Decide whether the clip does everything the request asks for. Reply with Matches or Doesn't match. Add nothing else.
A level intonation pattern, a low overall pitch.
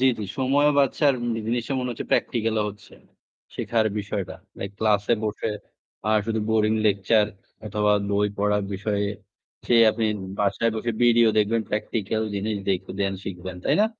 Matches